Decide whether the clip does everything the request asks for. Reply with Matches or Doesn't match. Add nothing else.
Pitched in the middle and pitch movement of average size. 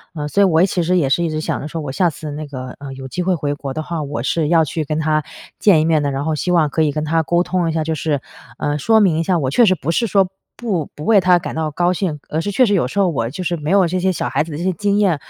Matches